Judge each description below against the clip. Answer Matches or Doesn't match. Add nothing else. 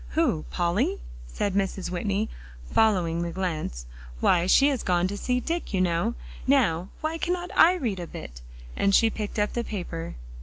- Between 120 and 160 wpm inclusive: Doesn't match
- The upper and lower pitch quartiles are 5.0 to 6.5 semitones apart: Matches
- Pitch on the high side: Matches